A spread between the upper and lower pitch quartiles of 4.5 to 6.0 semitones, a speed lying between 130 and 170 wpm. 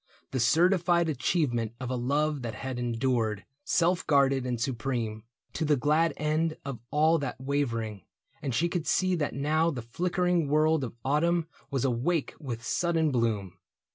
Yes: average, 5.0 semitones; average, 160 wpm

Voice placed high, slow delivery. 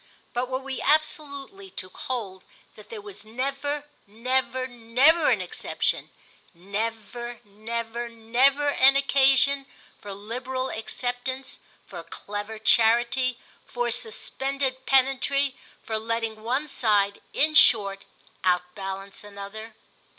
Yes: high, 240 Hz; slow, 105 wpm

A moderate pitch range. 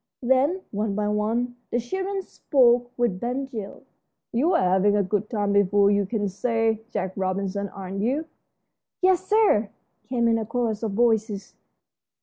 Yes: average, 3.4 semitones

